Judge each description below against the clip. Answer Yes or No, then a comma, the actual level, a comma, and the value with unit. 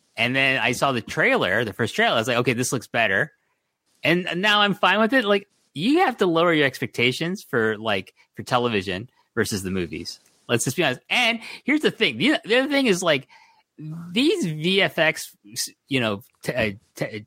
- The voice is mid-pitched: Yes, medium, 160 Hz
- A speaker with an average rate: Yes, average, 190 wpm